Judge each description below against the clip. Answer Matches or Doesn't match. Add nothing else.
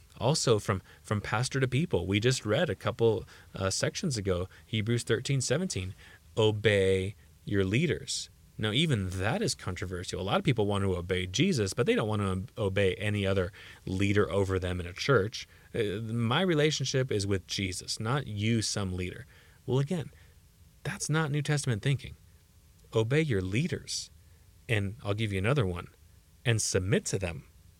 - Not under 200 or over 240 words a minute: Doesn't match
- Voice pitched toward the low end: Matches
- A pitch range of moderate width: Matches